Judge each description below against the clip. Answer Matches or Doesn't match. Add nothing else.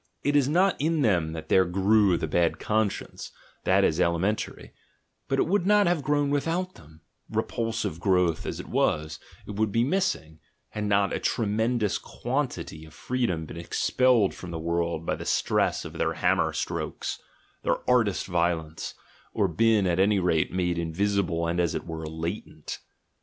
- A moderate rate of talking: Matches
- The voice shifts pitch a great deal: Matches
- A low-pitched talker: Matches